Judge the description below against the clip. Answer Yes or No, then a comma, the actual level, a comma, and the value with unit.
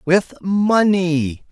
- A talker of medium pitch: Yes, medium, 175 Hz